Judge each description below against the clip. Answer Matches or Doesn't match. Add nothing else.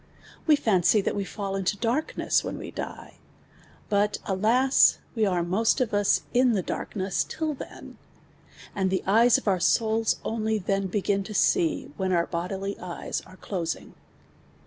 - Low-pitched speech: Doesn't match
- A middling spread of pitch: Matches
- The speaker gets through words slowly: Doesn't match